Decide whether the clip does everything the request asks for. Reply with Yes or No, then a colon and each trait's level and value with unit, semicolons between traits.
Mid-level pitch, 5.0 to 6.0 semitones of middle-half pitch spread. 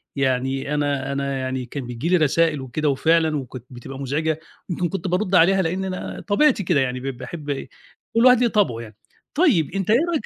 Yes: medium, 150 Hz; wide, 5.5 semitones